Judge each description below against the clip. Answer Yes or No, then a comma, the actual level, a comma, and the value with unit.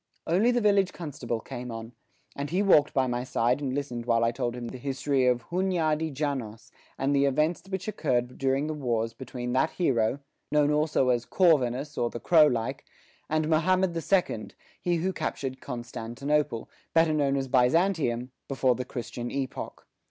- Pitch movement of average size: Yes, average, 4.3 semitones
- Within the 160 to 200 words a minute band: Yes, average, 175 wpm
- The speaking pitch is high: No, low, 135 Hz